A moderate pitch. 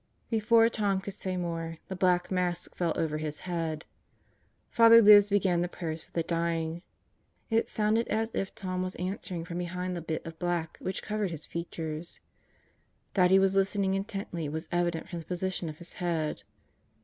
Yes: medium, 180 Hz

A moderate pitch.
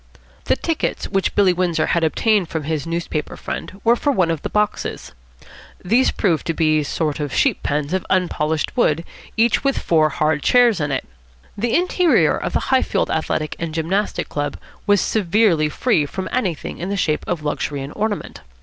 Yes: medium, 170 Hz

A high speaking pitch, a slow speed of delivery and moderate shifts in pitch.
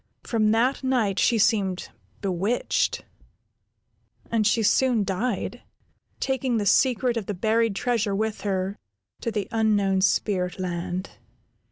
Yes: high, 215 Hz; slow, 125 wpm; average, 3.1 semitones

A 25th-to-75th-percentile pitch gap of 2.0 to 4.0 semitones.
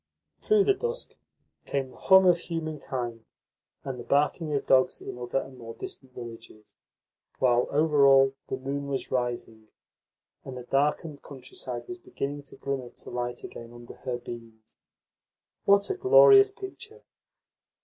No: average, 5.2 semitones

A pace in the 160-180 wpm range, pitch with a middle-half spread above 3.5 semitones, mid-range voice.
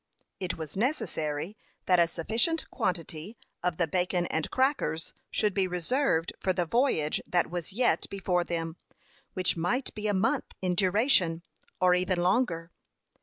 No: average, 150 wpm; average, 4.2 semitones; medium, 180 Hz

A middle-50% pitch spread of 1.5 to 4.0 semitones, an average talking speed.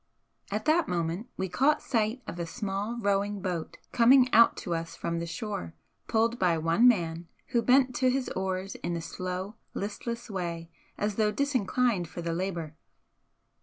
No: wide, 5.5 semitones; average, 165 wpm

